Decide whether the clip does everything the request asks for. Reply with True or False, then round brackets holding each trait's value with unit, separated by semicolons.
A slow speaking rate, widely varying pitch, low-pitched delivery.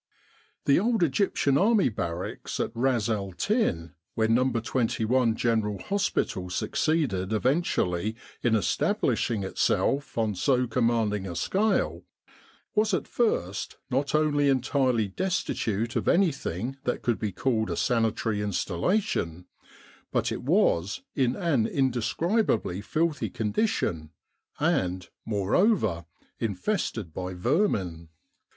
True (110 wpm; 6.4 semitones; 115 Hz)